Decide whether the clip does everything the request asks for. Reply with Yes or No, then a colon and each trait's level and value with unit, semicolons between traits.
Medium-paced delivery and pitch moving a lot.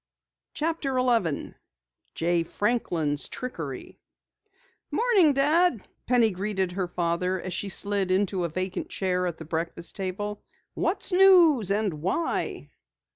No: slow, 120 wpm; wide, 6.3 semitones